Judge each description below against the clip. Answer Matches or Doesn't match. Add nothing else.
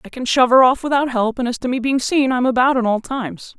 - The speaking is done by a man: Doesn't match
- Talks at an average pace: Doesn't match